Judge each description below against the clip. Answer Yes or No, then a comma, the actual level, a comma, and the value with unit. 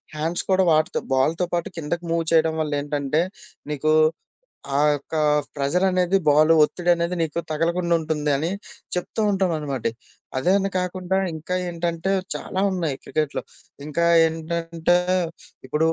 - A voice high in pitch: No, medium, 165 Hz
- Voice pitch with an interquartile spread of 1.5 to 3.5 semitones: Yes, narrow, 2.5 semitones